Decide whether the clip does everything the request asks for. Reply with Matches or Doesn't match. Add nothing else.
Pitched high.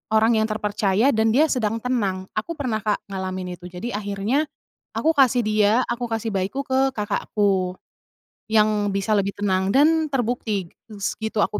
Matches